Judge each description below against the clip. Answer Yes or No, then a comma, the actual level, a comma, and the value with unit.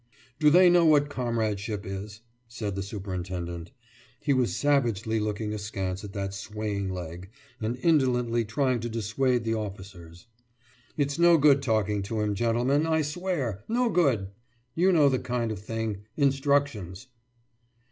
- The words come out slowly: No, average, 145 wpm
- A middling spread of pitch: No, wide, 5.8 semitones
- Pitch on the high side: No, low, 115 Hz